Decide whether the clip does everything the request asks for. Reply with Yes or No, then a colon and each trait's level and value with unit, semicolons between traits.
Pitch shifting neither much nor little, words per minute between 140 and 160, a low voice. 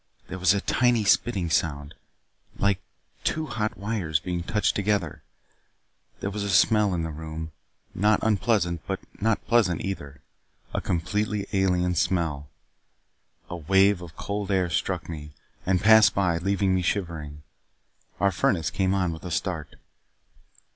Yes: average, 3.6 semitones; average, 145 wpm; very low, 95 Hz